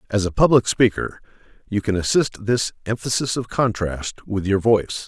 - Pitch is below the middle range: Yes, low, 105 Hz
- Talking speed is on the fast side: No, average, 165 wpm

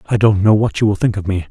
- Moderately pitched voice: No, low, 105 Hz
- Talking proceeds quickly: Yes, fast, 360 wpm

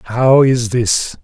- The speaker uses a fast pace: No, average, 145 wpm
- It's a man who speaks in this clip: Yes, male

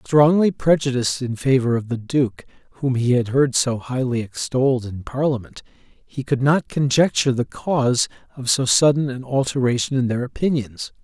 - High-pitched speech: No, low, 130 Hz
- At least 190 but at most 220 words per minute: No, average, 165 wpm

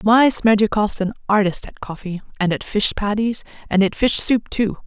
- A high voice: Yes, high, 210 Hz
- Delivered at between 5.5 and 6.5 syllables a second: No, 4.9 syllables/s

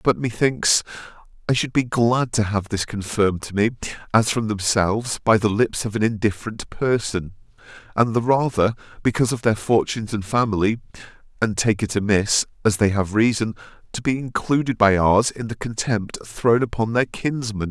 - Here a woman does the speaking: No, male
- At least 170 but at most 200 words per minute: Yes, average, 175 wpm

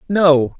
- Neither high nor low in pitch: Yes, medium, 165 Hz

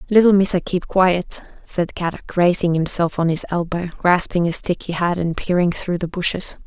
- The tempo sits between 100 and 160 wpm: No, average, 190 wpm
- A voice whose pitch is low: No, medium, 175 Hz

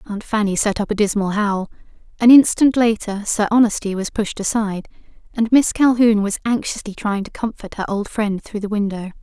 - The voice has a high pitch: Yes, high, 210 Hz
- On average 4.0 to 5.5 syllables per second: Yes, 5.4 syllables/s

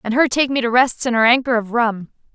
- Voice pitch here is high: Yes, high, 240 Hz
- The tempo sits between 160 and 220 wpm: No, fast, 280 wpm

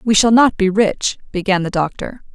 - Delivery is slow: No, fast, 205 wpm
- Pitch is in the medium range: No, high, 205 Hz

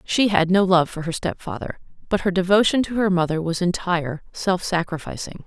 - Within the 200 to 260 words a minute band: No, average, 185 wpm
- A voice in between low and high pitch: Yes, medium, 180 Hz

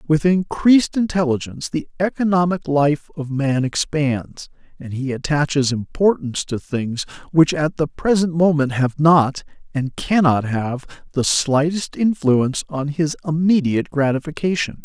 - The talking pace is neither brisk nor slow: No, slow, 130 wpm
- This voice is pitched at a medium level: Yes, medium, 150 Hz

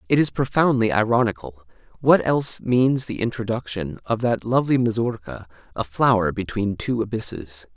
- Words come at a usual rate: No, slow, 130 wpm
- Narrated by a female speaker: No, male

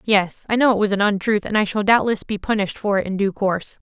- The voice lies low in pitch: No, high, 205 Hz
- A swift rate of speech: Yes, fast, 280 wpm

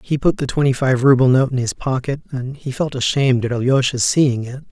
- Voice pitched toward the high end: No, low, 130 Hz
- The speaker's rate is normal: No, fast, 230 wpm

